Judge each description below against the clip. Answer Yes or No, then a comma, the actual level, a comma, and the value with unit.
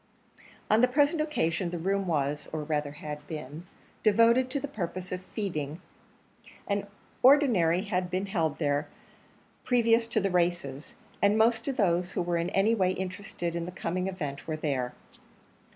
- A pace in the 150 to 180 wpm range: Yes, average, 165 wpm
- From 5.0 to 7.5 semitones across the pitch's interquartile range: Yes, average, 5.3 semitones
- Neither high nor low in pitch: Yes, medium, 180 Hz